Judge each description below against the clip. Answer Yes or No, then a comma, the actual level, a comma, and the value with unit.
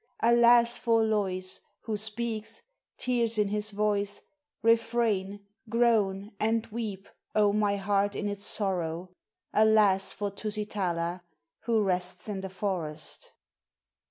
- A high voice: Yes, high, 210 Hz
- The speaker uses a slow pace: Yes, slow, 115 wpm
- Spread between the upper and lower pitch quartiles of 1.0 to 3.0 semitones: Yes, narrow, 2.4 semitones